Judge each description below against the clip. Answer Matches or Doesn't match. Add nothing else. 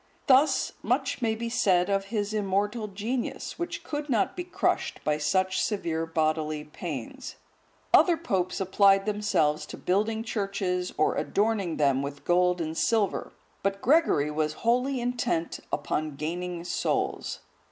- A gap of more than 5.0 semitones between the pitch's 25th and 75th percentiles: Matches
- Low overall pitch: Doesn't match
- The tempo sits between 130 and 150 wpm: Matches